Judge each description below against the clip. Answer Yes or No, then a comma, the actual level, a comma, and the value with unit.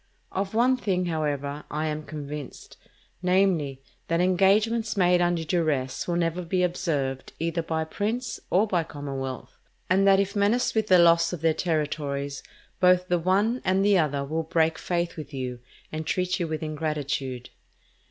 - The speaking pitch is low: No, medium, 170 Hz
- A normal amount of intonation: Yes, average, 3.7 semitones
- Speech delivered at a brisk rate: No, average, 160 wpm